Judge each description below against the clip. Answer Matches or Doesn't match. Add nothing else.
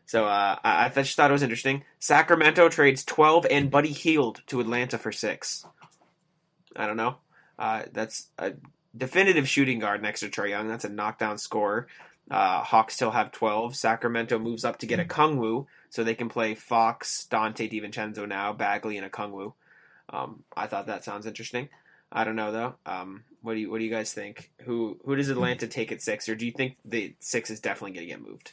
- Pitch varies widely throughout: Doesn't match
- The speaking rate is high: Matches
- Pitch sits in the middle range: Doesn't match